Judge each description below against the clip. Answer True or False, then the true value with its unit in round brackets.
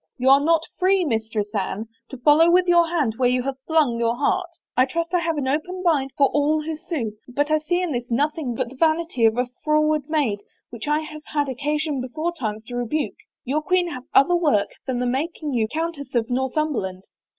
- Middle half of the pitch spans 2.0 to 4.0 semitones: False (4.5 semitones)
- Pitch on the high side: True (290 Hz)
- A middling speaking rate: False (215 wpm)